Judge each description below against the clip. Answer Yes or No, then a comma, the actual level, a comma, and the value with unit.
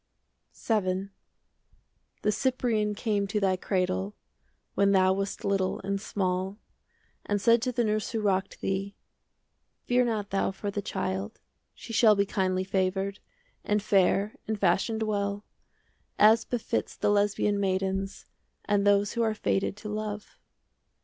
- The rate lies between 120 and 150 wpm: Yes, average, 145 wpm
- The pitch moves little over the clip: Yes, narrow, 1.7 semitones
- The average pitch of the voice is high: Yes, high, 200 Hz